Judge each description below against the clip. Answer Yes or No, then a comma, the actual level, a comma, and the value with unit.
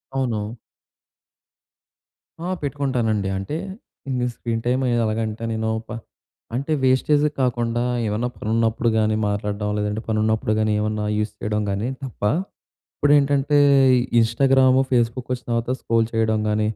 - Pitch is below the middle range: Yes, low, 115 Hz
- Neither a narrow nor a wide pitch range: Yes, average, 3.1 semitones